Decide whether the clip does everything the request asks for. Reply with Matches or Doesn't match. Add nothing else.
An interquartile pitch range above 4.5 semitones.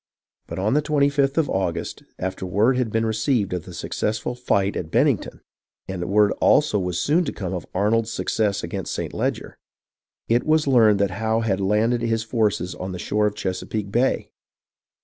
Doesn't match